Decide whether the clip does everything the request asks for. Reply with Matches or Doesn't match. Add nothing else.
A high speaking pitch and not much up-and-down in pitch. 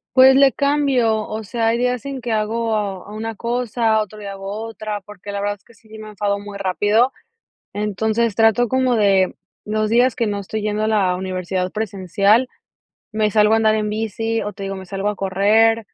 Matches